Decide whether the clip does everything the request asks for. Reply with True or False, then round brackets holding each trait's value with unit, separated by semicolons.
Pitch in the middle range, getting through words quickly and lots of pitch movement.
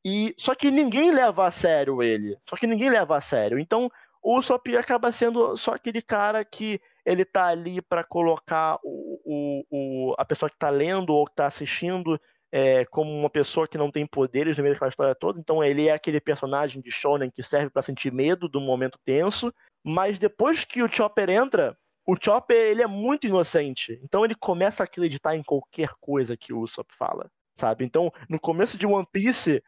True (165 Hz; 200 wpm; 7.2 semitones)